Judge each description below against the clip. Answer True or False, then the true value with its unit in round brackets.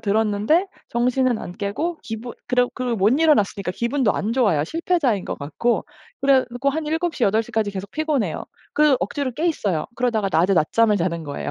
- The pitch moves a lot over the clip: True (5.7 semitones)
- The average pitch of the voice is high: True (230 Hz)